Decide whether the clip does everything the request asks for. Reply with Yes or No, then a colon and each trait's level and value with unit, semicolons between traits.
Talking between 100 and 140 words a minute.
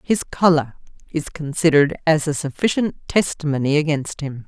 Yes: slow, 135 wpm